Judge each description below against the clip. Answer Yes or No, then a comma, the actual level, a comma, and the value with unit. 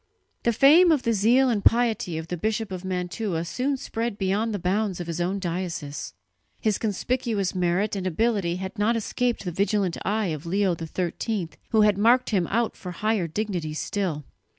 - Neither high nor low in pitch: No, high, 200 Hz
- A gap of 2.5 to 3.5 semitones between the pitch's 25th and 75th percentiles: No, average, 4.0 semitones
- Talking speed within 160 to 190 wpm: Yes, average, 180 wpm